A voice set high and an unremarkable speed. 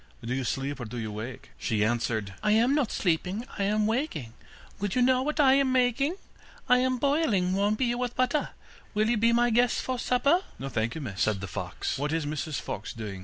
No: high, 210 Hz; fast, 220 wpm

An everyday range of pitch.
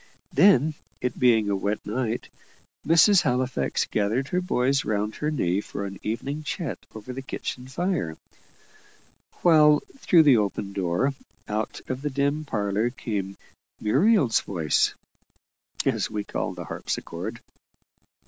No: wide, 6.0 semitones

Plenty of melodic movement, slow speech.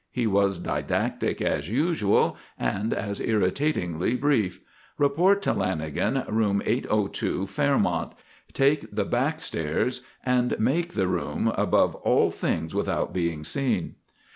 Yes: wide, 6.8 semitones; slow, 120 wpm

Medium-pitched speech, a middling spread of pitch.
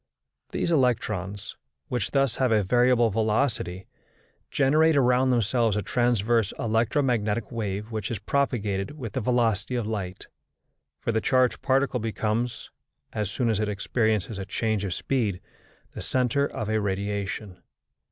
No: low, 115 Hz; average, 3.4 semitones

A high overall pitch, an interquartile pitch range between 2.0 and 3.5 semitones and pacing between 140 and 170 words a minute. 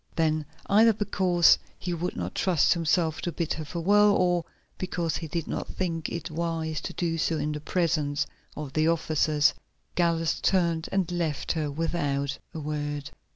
No: medium, 165 Hz; narrow, 2.4 semitones; average, 165 wpm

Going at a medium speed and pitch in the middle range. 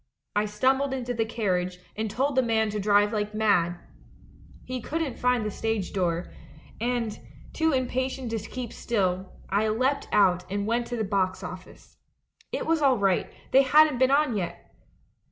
No: average, 170 wpm; high, 220 Hz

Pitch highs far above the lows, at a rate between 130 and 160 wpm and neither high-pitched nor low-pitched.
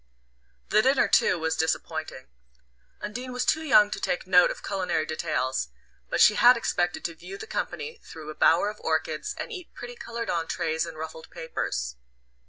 No: wide, 6.6 semitones; average, 175 wpm; medium, 180 Hz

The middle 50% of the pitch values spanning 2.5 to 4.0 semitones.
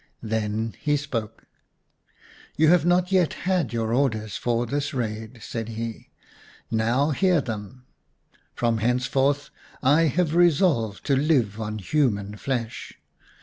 No: average, 5.0 semitones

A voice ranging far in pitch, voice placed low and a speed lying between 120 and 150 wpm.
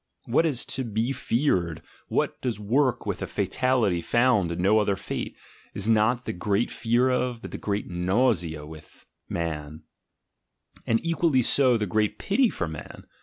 No: wide, 6.2 semitones; low, 110 Hz; average, 165 wpm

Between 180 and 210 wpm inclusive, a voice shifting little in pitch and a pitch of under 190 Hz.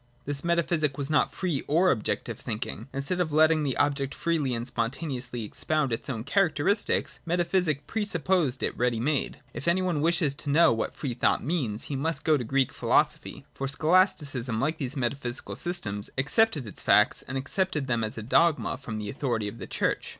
No: average, 190 wpm; average, 5.2 semitones; medium, 140 Hz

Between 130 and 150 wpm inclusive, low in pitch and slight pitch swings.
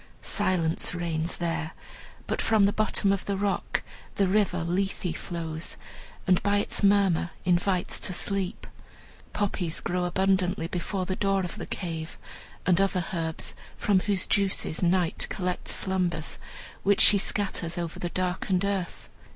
No: average, 145 wpm; medium, 185 Hz; narrow, 2.3 semitones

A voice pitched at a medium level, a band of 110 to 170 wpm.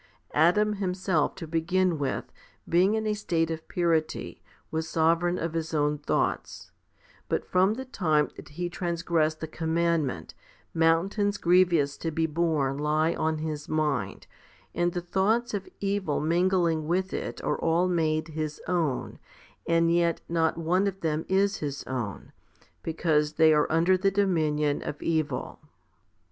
Yes: medium, 165 Hz; average, 150 wpm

